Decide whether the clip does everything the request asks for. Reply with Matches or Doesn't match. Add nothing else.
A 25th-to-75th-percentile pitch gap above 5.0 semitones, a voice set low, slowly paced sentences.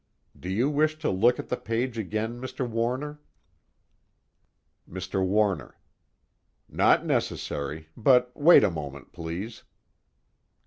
Matches